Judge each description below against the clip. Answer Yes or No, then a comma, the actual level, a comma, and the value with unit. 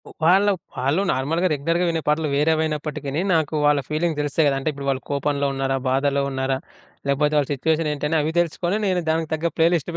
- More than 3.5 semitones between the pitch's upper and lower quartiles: No, average, 2.7 semitones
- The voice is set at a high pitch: No, medium, 150 Hz